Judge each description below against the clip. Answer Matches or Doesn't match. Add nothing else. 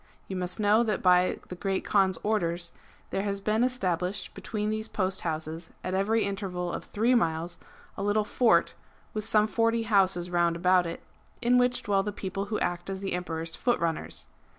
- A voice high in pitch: Matches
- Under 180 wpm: Doesn't match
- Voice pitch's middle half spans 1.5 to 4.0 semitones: Matches